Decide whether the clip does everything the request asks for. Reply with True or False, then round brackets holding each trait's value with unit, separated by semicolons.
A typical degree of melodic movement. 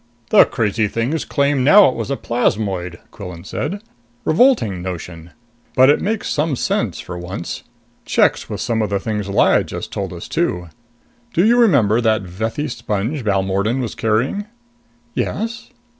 False (6.9 semitones)